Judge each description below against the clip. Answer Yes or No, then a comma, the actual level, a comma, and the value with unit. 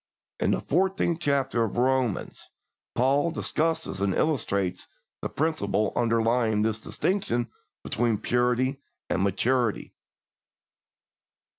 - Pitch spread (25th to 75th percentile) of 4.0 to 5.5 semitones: Yes, average, 4.4 semitones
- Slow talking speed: Yes, slow, 100 wpm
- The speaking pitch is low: Yes, low, 120 Hz